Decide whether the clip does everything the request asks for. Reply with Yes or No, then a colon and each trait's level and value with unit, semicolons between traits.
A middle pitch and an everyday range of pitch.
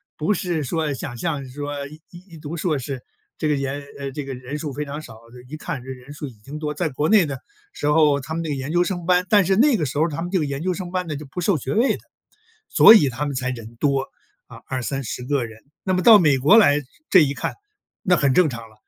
Yes: medium, 150 Hz; average, 4.1 semitones